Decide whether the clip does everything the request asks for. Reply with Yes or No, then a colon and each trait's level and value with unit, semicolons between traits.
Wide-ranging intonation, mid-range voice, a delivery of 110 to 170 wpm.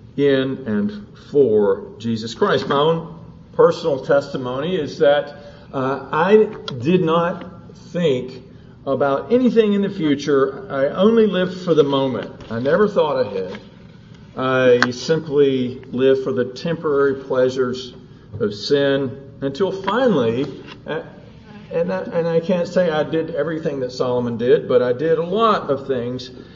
Yes: wide, 6.2 semitones; medium, 145 Hz; average, 140 wpm